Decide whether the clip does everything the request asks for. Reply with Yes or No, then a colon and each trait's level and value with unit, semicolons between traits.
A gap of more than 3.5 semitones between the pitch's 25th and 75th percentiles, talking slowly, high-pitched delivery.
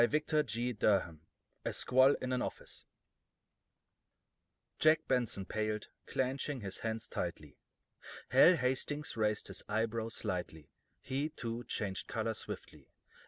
No: average, 3.9 semitones; slow, 115 wpm; low, 115 Hz